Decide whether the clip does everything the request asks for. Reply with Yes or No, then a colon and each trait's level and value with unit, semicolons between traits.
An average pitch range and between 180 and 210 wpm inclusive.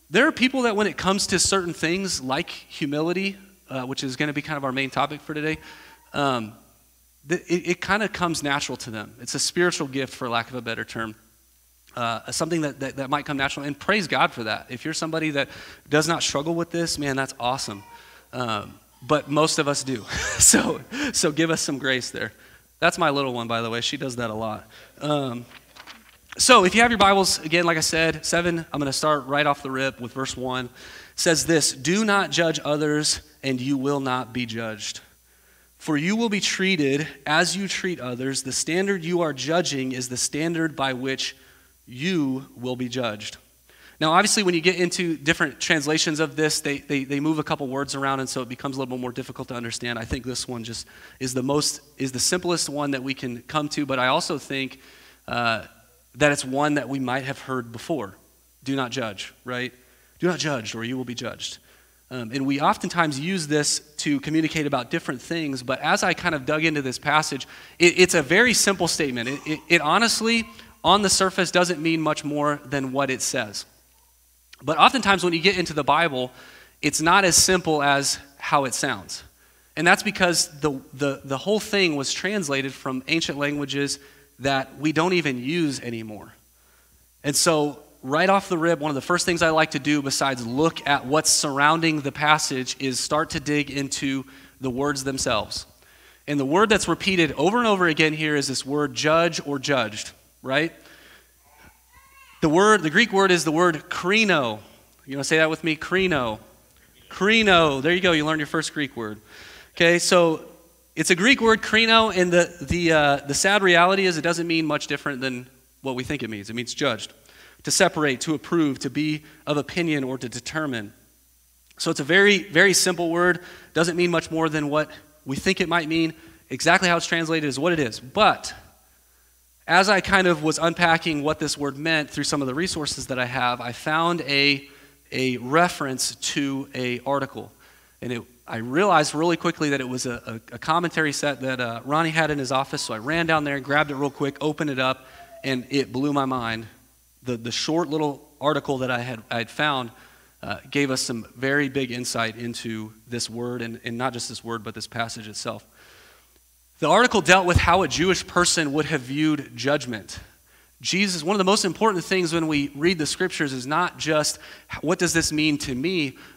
Yes: average, 4.5 semitones; fast, 205 wpm